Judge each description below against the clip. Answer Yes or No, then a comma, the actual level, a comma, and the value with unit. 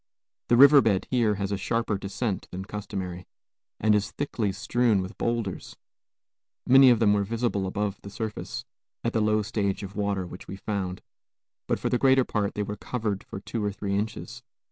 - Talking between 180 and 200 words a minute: Yes, average, 190 wpm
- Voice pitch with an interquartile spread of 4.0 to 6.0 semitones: No, average, 2.9 semitones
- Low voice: Yes, low, 105 Hz